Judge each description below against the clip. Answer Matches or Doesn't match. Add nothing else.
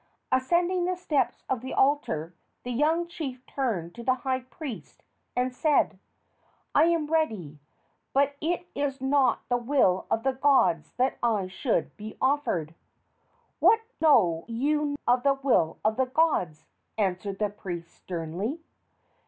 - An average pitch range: Doesn't match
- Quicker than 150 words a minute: Doesn't match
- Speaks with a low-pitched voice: Doesn't match